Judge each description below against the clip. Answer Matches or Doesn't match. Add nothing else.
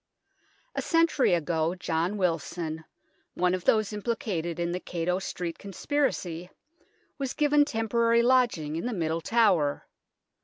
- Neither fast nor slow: Doesn't match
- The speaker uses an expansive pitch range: Matches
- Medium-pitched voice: Matches